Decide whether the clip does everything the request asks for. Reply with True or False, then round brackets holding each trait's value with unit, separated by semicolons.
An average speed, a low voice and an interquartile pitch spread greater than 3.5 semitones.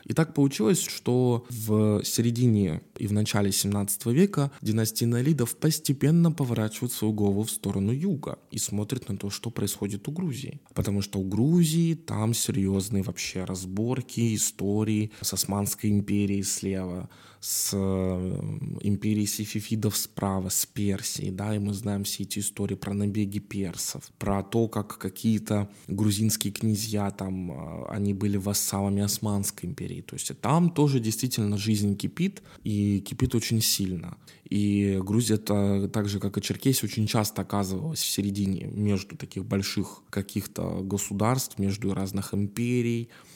False (140 wpm; 105 Hz; 2.7 semitones)